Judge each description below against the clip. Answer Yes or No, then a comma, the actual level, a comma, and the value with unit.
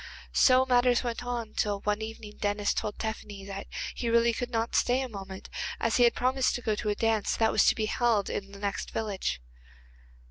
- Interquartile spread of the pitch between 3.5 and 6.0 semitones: No, average, 2.8 semitones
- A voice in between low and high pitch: No, high, 220 Hz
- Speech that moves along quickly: Yes, fast, 210 wpm